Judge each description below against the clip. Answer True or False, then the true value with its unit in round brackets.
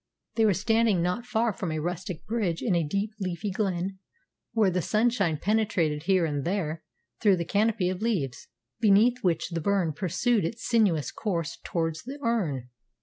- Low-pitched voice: False (190 Hz)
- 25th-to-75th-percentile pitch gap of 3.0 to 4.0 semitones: False (4.7 semitones)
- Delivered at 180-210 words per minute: False (170 wpm)